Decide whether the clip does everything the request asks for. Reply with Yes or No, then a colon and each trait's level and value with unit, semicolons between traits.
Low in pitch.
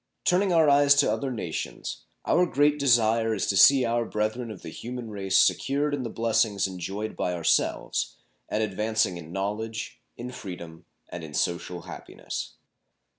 Yes: low, 110 Hz